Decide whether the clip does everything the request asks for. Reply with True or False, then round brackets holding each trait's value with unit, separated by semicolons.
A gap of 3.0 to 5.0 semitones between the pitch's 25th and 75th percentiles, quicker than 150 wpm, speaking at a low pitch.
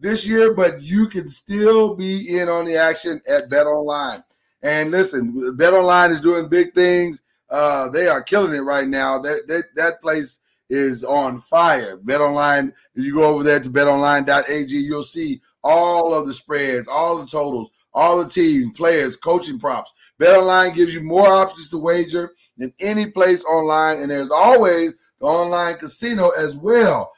False (4.2 semitones; 175 wpm; 165 Hz)